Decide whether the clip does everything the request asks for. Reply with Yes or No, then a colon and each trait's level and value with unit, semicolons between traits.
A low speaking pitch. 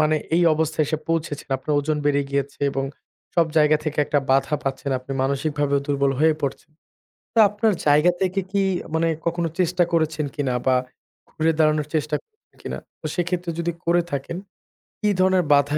No: medium, 155 Hz